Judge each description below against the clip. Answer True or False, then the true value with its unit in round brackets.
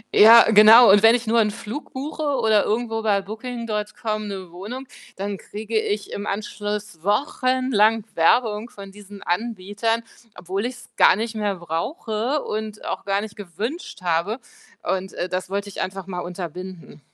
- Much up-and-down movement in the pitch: False (2.8 semitones)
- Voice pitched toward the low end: False (210 Hz)